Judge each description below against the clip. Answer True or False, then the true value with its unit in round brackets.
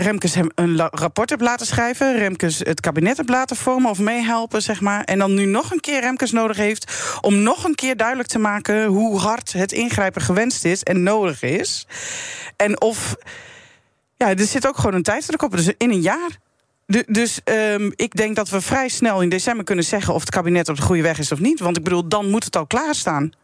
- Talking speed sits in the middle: False (225 wpm)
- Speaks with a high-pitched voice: True (215 Hz)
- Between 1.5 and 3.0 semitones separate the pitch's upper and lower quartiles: False (4.7 semitones)